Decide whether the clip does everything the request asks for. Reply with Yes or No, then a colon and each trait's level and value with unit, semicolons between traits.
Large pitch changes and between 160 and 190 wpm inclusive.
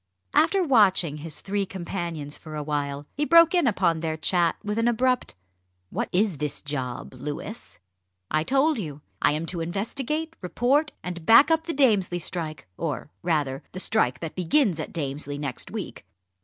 Yes: wide, 7.7 semitones; average, 170 wpm